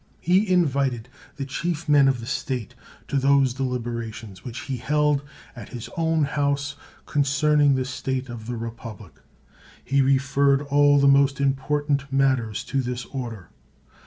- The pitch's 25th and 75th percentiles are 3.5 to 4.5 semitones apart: No, narrow, 2.6 semitones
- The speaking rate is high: No, average, 145 wpm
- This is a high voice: No, low, 135 Hz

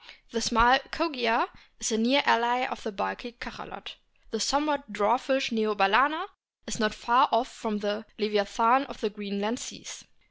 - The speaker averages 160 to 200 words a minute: Yes, average, 165 wpm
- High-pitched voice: Yes, high, 230 Hz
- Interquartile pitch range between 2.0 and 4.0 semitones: Yes, average, 3.5 semitones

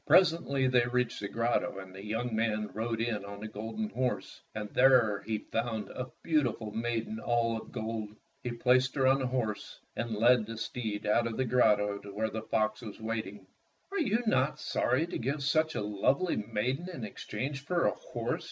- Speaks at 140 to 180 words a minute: No, average, 195 wpm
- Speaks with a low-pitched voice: Yes, low, 115 Hz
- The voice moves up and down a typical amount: Yes, average, 3.3 semitones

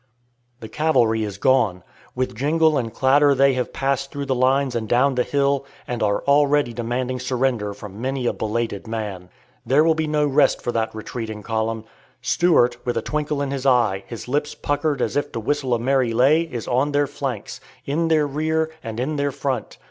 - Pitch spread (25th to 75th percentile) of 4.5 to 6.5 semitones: No, average, 3.8 semitones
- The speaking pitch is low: Yes, low, 130 Hz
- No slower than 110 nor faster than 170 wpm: No, average, 195 wpm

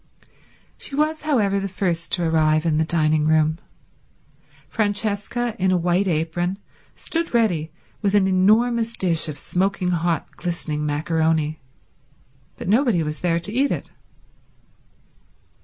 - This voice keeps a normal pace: No, slow, 130 wpm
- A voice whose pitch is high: No, medium, 180 Hz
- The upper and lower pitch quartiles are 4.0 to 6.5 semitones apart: Yes, average, 4.6 semitones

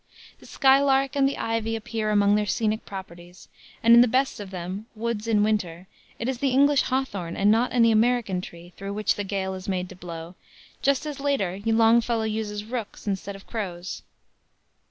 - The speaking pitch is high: Yes, high, 215 Hz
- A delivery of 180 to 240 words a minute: Yes, average, 185 wpm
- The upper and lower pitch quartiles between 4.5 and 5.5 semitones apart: No, average, 3.8 semitones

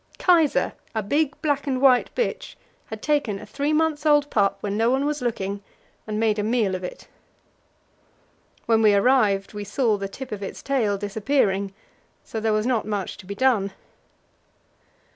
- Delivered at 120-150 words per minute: No, average, 175 wpm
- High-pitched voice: Yes, high, 220 Hz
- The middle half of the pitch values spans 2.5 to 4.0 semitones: No, average, 5.3 semitones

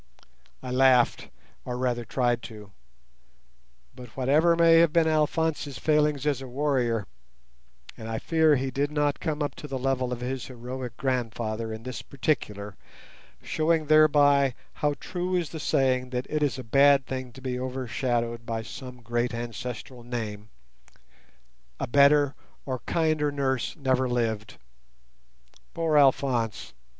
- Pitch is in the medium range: No, low, 130 Hz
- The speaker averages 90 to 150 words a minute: Yes, average, 145 wpm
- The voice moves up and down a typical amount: Yes, average, 3.4 semitones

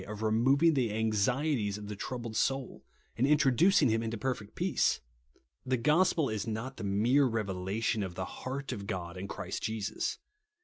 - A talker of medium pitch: No, low, 115 Hz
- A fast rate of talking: No, average, 165 wpm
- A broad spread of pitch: No, average, 4.4 semitones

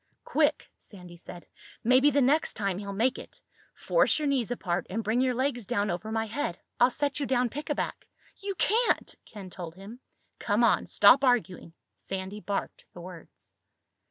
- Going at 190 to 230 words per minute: No, average, 170 wpm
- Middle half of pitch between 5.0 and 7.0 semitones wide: Yes, average, 5.3 semitones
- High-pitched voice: Yes, high, 225 Hz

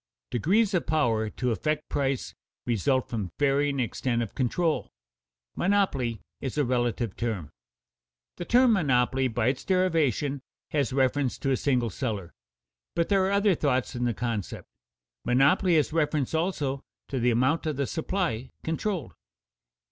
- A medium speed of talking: Yes, average, 145 wpm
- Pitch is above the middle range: No, low, 135 Hz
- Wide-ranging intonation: No, average, 4.9 semitones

